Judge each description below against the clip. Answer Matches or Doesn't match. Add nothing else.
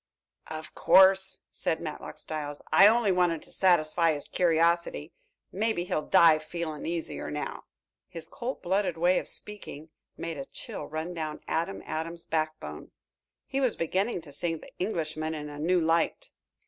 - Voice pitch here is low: Doesn't match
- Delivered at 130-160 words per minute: Matches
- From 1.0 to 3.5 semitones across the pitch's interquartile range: Matches